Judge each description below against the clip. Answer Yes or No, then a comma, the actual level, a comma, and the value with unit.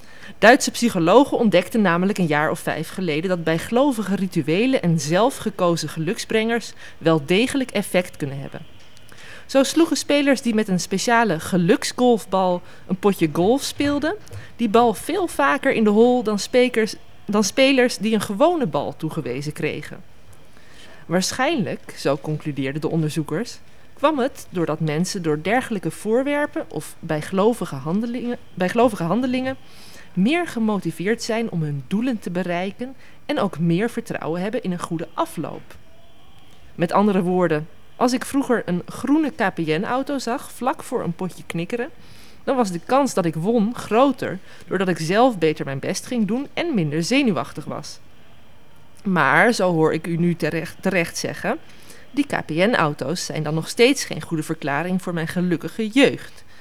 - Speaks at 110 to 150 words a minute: Yes, average, 145 wpm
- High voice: Yes, high, 195 Hz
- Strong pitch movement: Yes, wide, 6.7 semitones